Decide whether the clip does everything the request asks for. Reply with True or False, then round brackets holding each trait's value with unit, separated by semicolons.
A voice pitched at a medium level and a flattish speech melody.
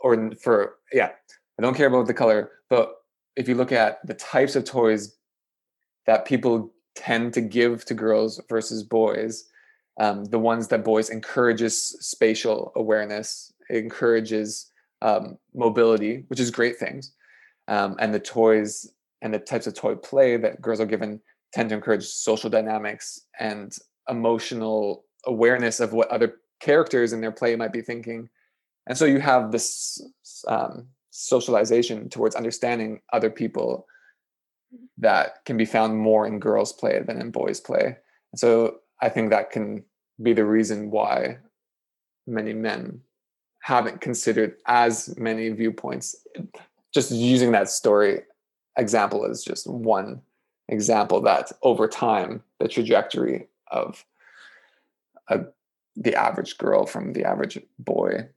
False (115 Hz; 1.5 semitones)